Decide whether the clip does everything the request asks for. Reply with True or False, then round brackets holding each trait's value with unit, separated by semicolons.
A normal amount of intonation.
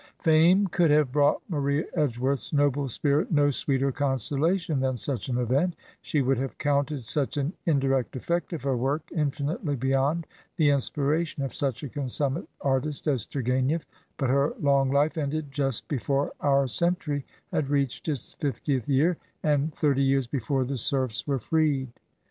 False (2.2 semitones)